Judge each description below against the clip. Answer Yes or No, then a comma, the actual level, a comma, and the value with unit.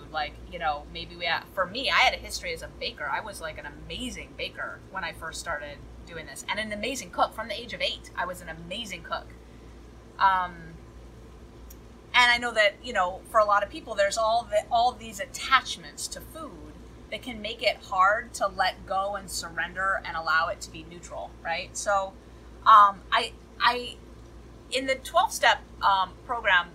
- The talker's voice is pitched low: No, high, 210 Hz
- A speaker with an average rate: Yes, average, 195 wpm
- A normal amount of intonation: No, wide, 6.6 semitones